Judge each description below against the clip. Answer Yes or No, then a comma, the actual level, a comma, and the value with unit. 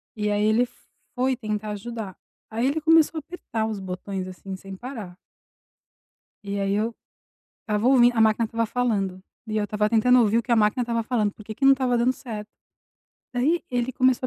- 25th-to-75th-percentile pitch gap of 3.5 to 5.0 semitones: No, average, 3.0 semitones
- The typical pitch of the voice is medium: No, high, 225 Hz